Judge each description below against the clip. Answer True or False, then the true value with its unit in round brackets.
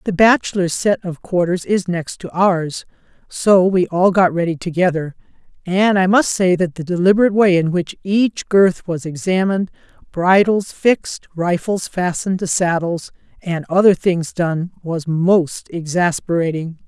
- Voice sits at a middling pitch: True (180 Hz)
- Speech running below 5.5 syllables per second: True (4.4 syllables/s)